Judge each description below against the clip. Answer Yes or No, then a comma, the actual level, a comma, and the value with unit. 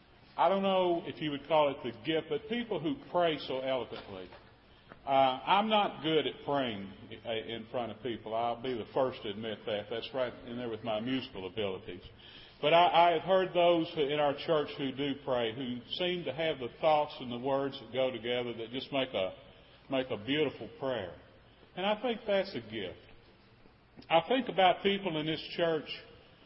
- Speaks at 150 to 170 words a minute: No, average, 195 wpm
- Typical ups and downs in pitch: No, wide, 5.9 semitones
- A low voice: No, medium, 145 Hz